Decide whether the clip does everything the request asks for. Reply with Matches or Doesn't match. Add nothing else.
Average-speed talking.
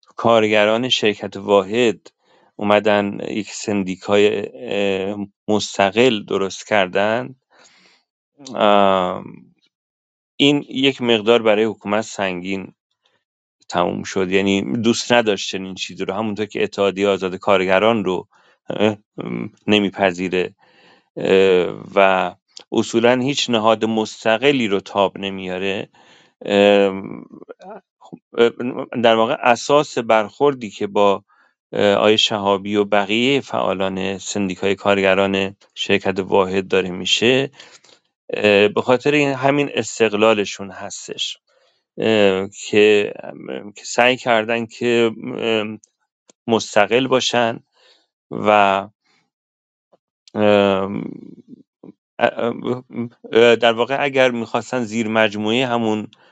Doesn't match